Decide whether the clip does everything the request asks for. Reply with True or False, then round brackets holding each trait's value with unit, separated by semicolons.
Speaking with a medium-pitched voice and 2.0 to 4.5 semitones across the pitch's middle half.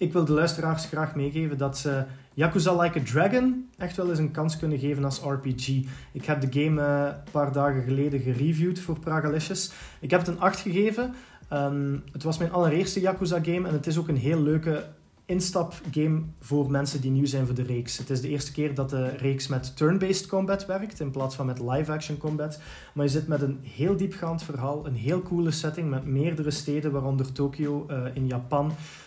True (150 Hz; 3.3 semitones)